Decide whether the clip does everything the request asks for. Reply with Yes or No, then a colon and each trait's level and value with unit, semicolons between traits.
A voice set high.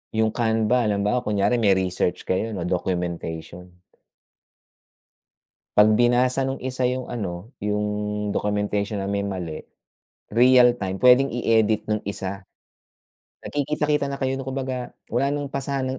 No: low, 110 Hz